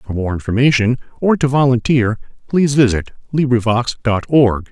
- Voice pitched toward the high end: No, low, 125 Hz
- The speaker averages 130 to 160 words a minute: Yes, average, 140 wpm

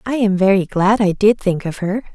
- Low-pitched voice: No, high, 200 Hz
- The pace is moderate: No, fast, 250 wpm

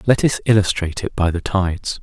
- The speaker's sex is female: No, male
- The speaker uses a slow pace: No, fast, 205 wpm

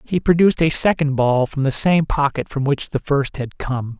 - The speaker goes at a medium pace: No, fast, 225 wpm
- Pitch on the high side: No, medium, 140 Hz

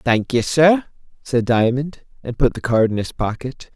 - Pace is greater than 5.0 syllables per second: No, 4.5 syllables/s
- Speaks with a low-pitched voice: Yes, low, 130 Hz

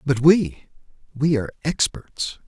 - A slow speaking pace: Yes, slow, 120 wpm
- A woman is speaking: No, male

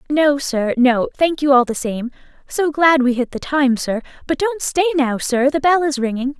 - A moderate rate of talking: No, fast, 225 wpm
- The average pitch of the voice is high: Yes, very high, 275 Hz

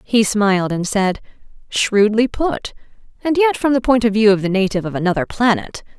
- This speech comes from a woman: Yes, female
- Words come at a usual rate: Yes, average, 190 wpm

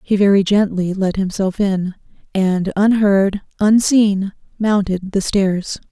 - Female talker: Yes, female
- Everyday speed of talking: No, slow, 120 wpm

